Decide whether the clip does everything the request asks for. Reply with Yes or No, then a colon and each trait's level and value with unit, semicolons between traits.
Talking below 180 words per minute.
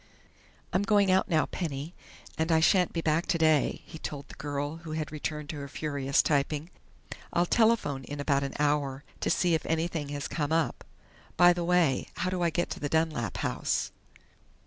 No: average, 190 wpm